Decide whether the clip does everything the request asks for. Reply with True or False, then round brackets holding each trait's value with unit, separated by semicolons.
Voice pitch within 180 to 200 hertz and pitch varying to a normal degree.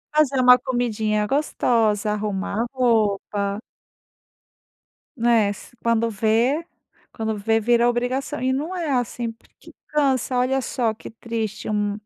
False (230 Hz; 3.1 semitones)